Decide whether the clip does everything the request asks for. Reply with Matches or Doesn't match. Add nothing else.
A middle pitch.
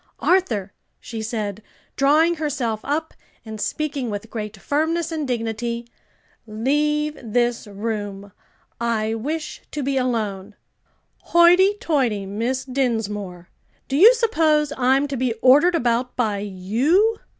Doesn't match